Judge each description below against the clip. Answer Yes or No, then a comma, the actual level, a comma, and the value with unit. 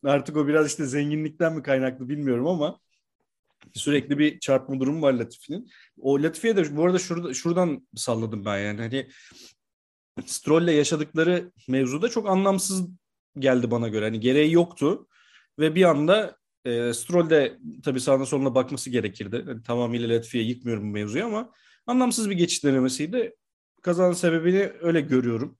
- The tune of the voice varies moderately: No, wide, 5.9 semitones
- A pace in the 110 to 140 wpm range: No, fast, 150 wpm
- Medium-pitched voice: Yes, medium, 145 Hz